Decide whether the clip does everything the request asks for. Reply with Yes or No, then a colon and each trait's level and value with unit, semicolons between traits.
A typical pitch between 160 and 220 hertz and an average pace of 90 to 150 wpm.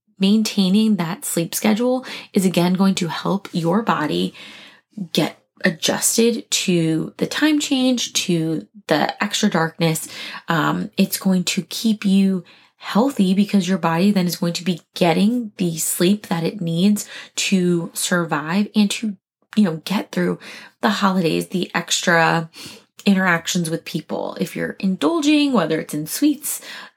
Yes: high, 190 Hz; average, 140 wpm